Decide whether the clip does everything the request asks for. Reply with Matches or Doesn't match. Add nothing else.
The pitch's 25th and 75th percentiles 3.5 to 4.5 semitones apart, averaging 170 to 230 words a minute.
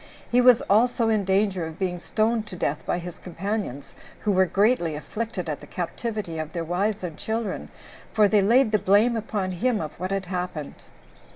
Matches